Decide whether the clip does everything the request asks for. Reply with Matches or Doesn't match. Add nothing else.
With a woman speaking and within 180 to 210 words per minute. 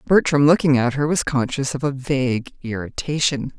Doesn't match